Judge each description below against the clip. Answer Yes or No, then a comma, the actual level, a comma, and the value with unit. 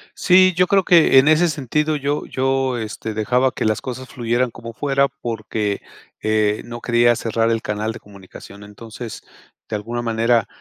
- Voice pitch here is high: No, low, 120 Hz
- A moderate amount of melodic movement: Yes, average, 3.6 semitones